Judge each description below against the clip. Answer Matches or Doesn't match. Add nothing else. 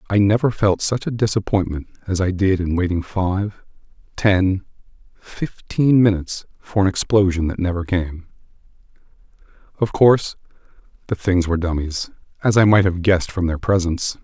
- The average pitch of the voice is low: Matches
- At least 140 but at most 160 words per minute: Matches